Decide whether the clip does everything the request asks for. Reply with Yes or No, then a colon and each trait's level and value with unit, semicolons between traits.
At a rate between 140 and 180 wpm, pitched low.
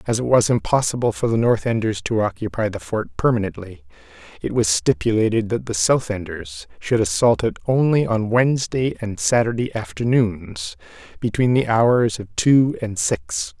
Yes: average, 160 wpm; low, 115 Hz